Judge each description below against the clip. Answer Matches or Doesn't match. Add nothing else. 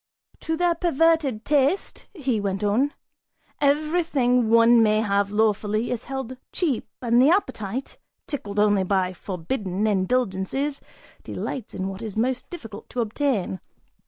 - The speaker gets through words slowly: Matches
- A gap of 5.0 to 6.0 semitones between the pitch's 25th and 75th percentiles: Matches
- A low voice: Doesn't match